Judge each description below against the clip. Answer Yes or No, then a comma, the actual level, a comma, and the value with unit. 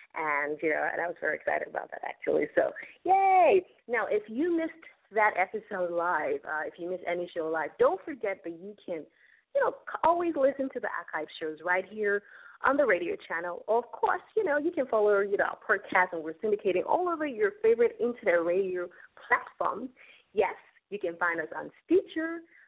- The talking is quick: No, average, 195 wpm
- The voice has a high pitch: Yes, high, 215 Hz